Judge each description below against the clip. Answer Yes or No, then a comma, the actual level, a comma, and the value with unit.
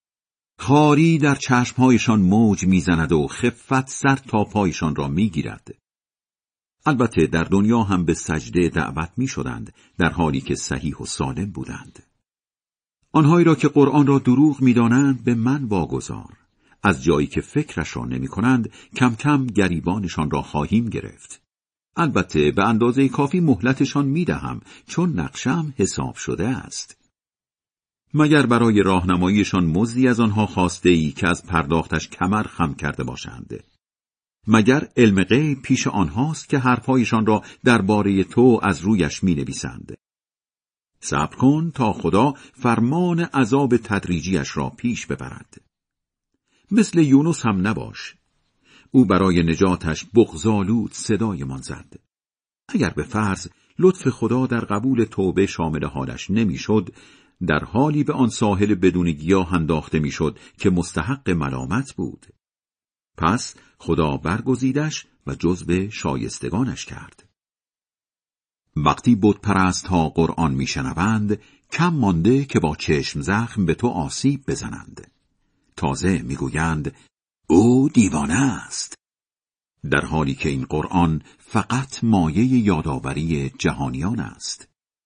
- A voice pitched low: Yes, low, 105 Hz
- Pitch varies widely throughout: Yes, wide, 7.3 semitones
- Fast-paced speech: No, average, 125 wpm